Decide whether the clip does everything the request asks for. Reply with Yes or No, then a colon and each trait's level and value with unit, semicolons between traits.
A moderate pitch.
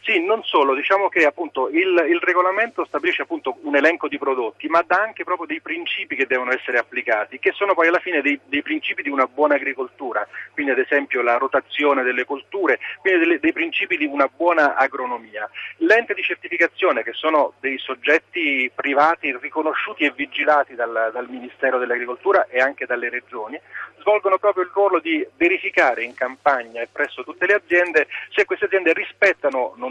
Yes: medium, 165 Hz